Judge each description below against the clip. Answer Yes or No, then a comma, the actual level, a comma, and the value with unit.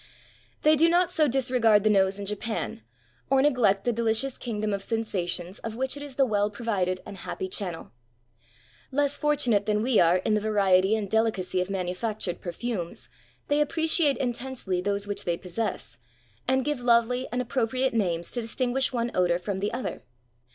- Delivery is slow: No, average, 180 wpm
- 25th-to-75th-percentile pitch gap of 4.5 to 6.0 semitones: Yes, average, 4.8 semitones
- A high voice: Yes, high, 220 Hz